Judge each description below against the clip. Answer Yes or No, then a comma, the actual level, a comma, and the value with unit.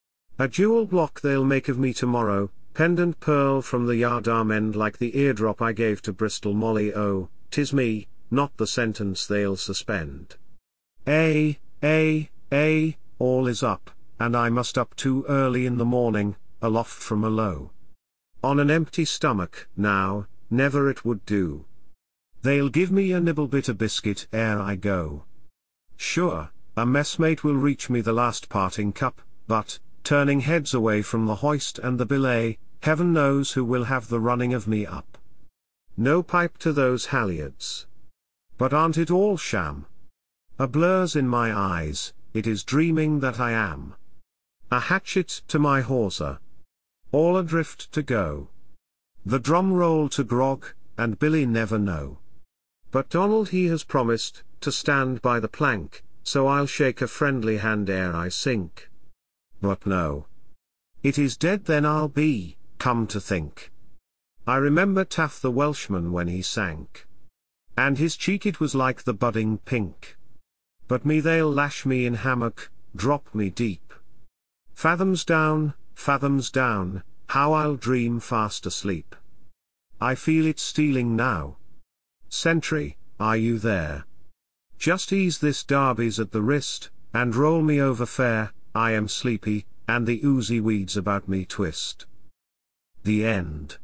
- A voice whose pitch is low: Yes, low, 120 Hz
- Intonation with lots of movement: Yes, wide, 6.1 semitones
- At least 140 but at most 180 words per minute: Yes, average, 150 wpm